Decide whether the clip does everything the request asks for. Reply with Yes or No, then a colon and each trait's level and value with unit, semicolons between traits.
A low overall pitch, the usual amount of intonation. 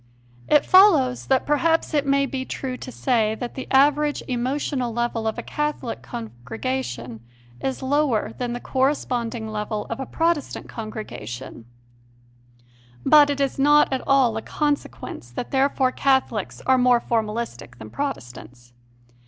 No: very high, 250 Hz; average, 4.5 semitones